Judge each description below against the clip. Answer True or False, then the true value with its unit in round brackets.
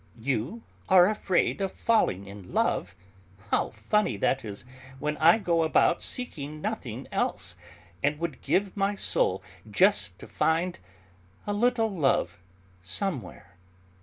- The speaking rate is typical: False (130 wpm)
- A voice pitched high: False (165 Hz)